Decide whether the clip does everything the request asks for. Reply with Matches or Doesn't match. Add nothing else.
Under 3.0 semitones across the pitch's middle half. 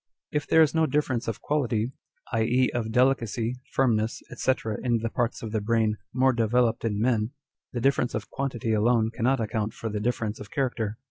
Matches